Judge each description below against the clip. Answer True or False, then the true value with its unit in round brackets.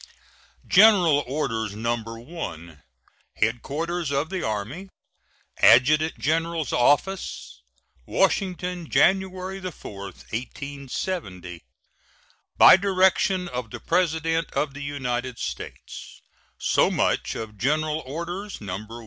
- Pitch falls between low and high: True (150 Hz)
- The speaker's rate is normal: False (95 wpm)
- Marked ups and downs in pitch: True (7.0 semitones)